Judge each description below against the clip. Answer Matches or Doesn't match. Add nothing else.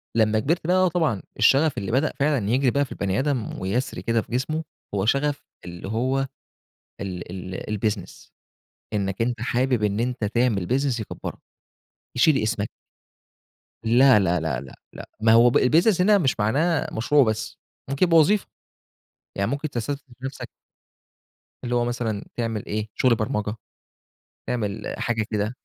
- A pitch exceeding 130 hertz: Doesn't match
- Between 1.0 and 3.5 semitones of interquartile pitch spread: Doesn't match